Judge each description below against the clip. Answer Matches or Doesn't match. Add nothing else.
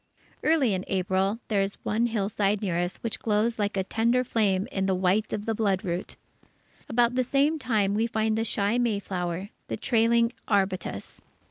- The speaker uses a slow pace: Doesn't match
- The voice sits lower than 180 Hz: Doesn't match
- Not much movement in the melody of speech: Doesn't match